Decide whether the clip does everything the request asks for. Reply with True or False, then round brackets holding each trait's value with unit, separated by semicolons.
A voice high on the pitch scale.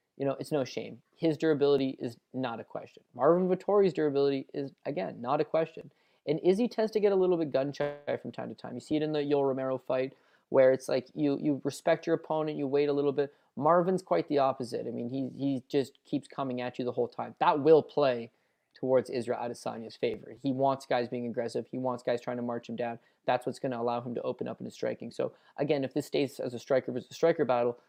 False (135 Hz)